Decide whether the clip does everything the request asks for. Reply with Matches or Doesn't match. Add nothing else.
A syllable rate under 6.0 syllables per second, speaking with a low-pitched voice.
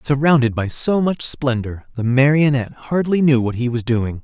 Matches